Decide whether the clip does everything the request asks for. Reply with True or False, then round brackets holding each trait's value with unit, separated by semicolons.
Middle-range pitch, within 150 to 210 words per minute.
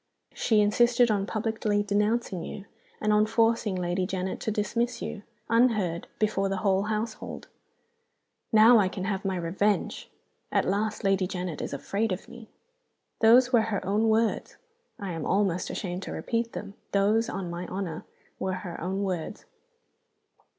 False (205 Hz; 155 wpm)